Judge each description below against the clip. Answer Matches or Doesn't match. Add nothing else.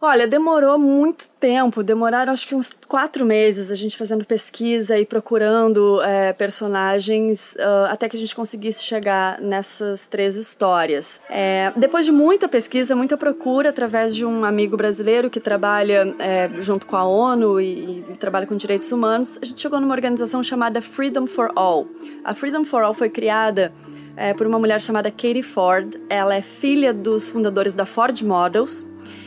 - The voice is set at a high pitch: Matches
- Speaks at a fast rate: Doesn't match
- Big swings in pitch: Doesn't match